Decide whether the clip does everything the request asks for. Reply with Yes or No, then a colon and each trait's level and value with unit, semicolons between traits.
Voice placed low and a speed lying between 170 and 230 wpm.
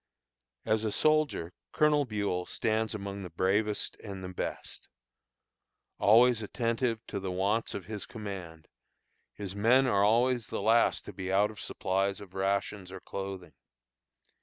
No: low, 100 Hz; average, 145 wpm